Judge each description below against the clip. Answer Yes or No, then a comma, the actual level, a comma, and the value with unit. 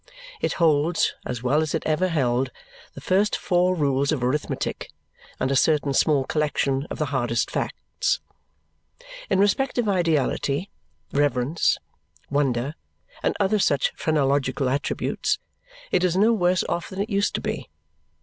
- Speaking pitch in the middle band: Yes, medium, 150 Hz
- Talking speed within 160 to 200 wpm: No, average, 145 wpm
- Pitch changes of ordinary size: Yes, average, 5.0 semitones